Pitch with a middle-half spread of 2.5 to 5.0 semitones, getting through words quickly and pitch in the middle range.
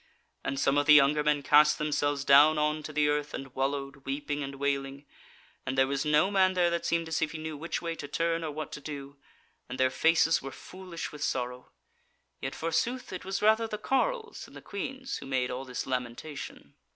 Yes: average, 3.3 semitones; fast, 210 wpm; medium, 150 Hz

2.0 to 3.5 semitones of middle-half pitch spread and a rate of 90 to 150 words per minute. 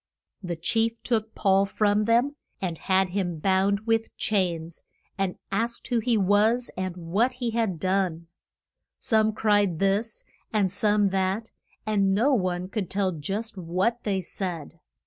Yes: average, 3.1 semitones; average, 145 wpm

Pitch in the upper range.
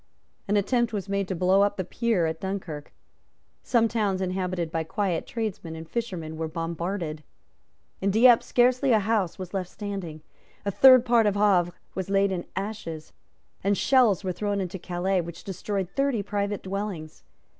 Yes: high, 195 Hz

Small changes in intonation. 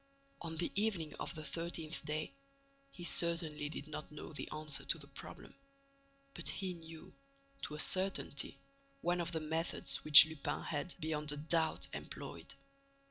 Yes: narrow, 2.0 semitones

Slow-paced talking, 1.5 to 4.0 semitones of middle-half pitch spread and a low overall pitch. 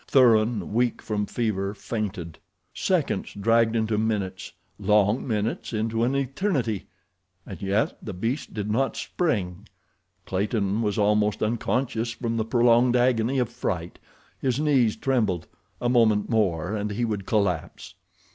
Yes: slow, 130 wpm; average, 2.8 semitones; low, 110 Hz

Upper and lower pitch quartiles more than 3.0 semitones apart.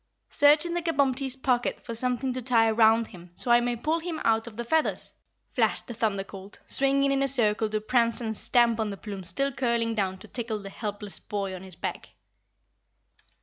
Yes: average, 3.9 semitones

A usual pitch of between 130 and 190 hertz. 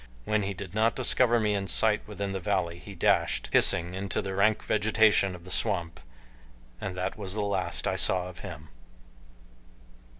No: low, 100 Hz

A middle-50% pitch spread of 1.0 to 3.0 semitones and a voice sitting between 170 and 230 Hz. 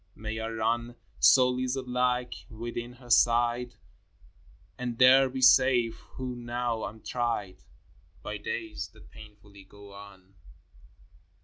No: narrow, 2.5 semitones; low, 120 Hz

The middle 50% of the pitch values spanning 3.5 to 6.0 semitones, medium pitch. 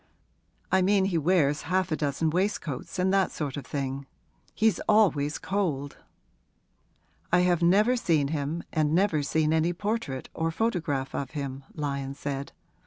Yes: average, 4.8 semitones; medium, 160 Hz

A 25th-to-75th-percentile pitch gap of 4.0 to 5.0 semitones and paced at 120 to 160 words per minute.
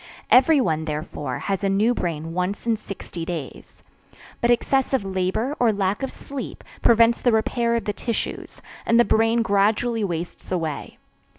Yes: average, 4.6 semitones; average, 155 wpm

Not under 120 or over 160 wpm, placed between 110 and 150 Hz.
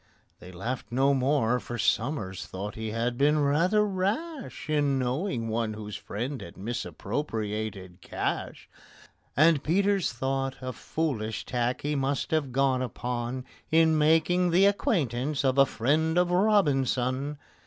Yes: slow, 135 wpm; low, 135 Hz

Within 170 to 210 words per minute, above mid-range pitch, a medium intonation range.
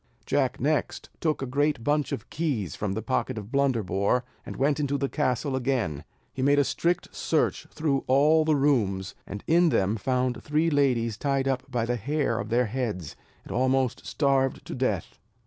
No: average, 180 wpm; low, 130 Hz; average, 3.9 semitones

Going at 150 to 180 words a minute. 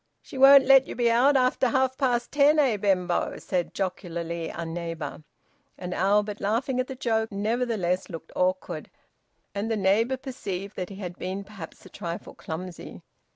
Yes: average, 165 wpm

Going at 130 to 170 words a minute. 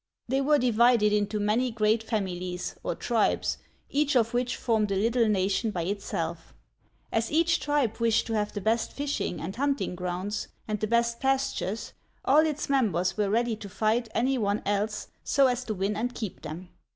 No: average, 190 wpm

